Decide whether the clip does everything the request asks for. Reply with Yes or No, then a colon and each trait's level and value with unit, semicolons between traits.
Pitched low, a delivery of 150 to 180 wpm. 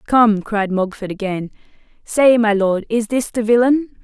No: high, 220 Hz; average, 165 wpm